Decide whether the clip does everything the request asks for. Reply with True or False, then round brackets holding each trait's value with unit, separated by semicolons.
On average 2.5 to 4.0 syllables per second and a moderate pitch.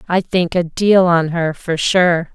True (3.7 syllables/s; 175 Hz)